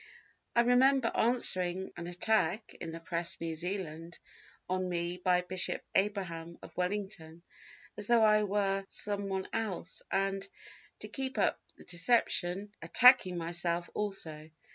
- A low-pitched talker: No, medium, 185 Hz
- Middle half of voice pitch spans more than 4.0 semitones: No, average, 3.2 semitones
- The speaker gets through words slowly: Yes, slow, 130 wpm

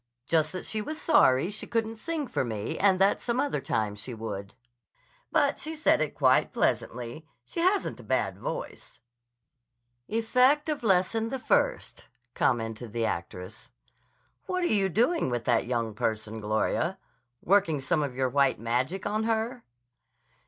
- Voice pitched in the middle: Yes, medium, 170 Hz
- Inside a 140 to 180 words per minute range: Yes, average, 155 wpm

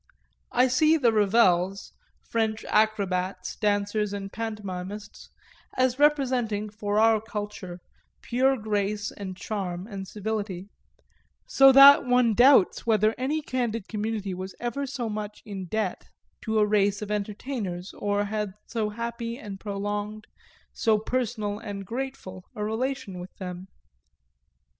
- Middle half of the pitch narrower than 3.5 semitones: Yes, average, 2.8 semitones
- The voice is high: Yes, high, 210 Hz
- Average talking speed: No, slow, 130 wpm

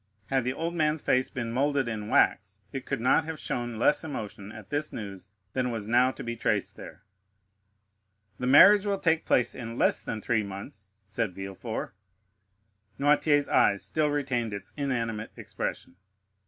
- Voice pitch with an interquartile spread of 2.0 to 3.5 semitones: No, average, 5.2 semitones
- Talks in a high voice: No, low, 120 Hz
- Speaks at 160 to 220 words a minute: Yes, average, 165 wpm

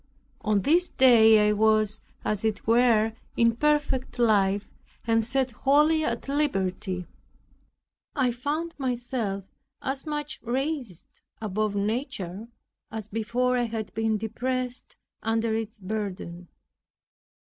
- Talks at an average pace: No, slow, 115 wpm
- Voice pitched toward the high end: Yes, high, 225 Hz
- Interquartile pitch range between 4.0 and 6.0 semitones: No, average, 3.4 semitones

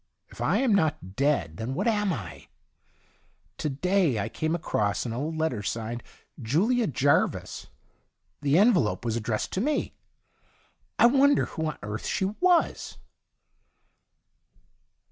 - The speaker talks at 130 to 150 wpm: Yes, average, 140 wpm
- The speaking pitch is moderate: Yes, medium, 150 Hz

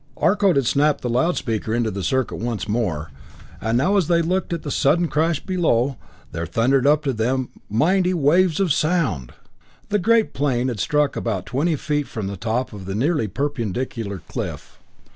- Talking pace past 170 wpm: Yes, average, 180 wpm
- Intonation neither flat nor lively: No, wide, 6.4 semitones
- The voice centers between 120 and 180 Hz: Yes, low, 135 Hz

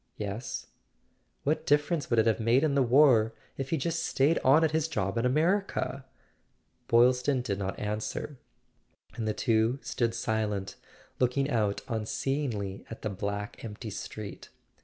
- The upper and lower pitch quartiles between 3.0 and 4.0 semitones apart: No, average, 4.4 semitones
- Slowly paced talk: No, average, 150 wpm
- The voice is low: Yes, low, 120 Hz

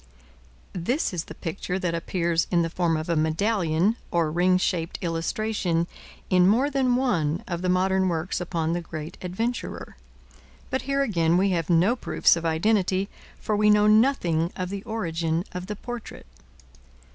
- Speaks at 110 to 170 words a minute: Yes, average, 165 wpm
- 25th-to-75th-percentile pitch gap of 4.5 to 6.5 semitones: No, average, 4.0 semitones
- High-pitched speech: No, medium, 180 Hz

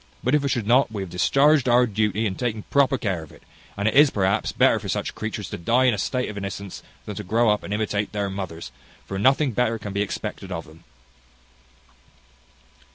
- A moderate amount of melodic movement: Yes, average, 4.0 semitones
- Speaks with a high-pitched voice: No, low, 105 Hz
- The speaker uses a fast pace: Yes, fast, 220 wpm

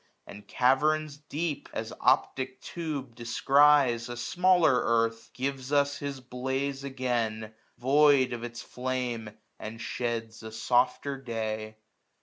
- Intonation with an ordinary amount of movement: Yes, average, 3.4 semitones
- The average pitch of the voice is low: Yes, low, 130 Hz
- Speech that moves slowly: Yes, slow, 125 wpm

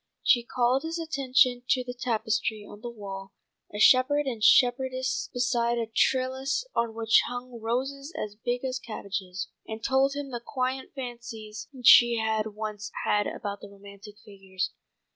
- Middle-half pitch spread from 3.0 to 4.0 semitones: Yes, average, 3.3 semitones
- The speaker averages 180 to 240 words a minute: No, average, 155 wpm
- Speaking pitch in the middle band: No, high, 240 Hz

